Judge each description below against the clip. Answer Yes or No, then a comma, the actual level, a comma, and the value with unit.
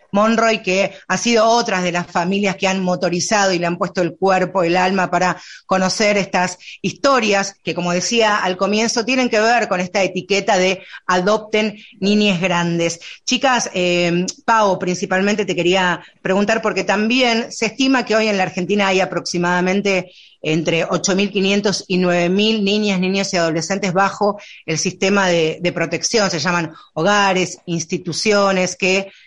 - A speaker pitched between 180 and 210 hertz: Yes, high, 190 Hz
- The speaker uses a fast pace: No, average, 155 wpm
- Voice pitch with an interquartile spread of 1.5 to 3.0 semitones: Yes, narrow, 2.4 semitones